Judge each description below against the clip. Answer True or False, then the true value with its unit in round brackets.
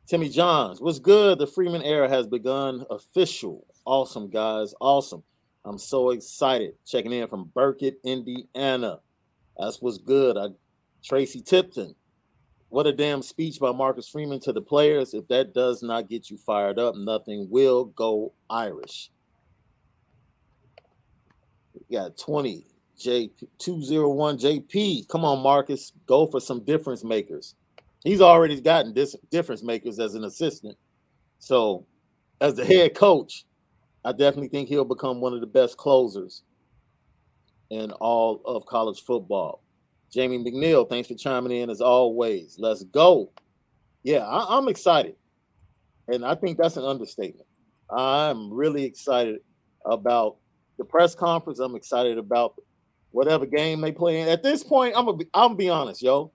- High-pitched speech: False (135 Hz)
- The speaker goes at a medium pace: True (145 wpm)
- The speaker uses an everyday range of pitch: True (4.6 semitones)